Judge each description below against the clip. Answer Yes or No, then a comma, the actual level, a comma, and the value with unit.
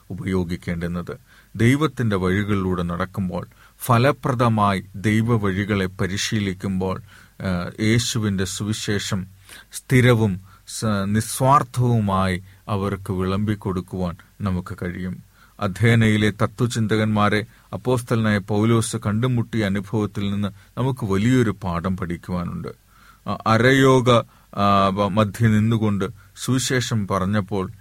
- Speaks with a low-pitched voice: Yes, low, 105 Hz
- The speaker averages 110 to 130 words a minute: No, average, 70 wpm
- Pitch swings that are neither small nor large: Yes, average, 3.0 semitones